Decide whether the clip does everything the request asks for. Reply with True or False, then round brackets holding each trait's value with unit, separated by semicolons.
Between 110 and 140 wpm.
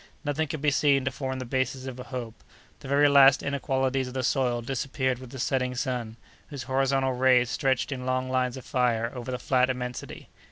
False (205 wpm)